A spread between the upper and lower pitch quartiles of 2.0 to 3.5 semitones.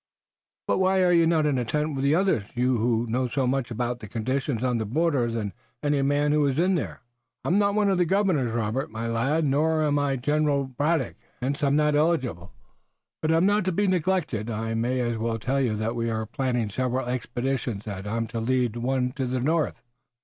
No: average, 4.6 semitones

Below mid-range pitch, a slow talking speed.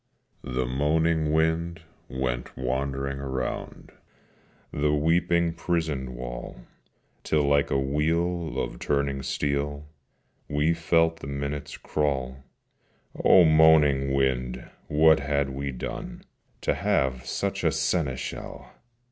Yes: very low, 70 Hz; slow, 105 wpm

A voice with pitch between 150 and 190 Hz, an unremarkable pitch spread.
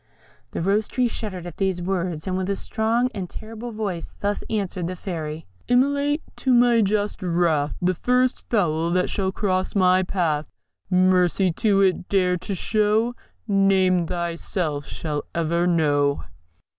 Yes: medium, 185 Hz; average, 3.6 semitones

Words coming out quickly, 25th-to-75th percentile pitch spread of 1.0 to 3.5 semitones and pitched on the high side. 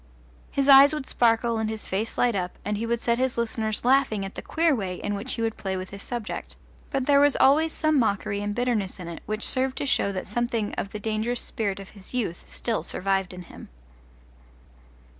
No: fast, 215 wpm; average, 4.0 semitones; high, 225 Hz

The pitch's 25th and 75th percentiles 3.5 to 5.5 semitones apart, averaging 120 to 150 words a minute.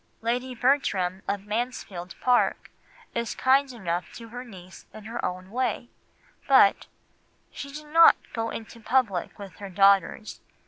Yes: average, 4.6 semitones; average, 140 wpm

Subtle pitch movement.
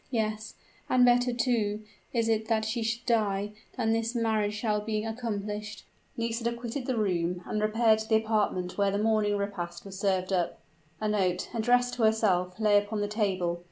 Yes: narrow, 2.0 semitones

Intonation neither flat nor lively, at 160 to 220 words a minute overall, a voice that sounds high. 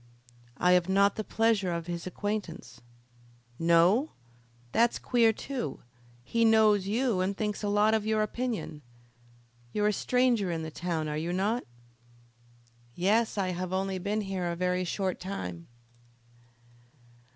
No: average, 3.6 semitones; average, 140 wpm; high, 195 Hz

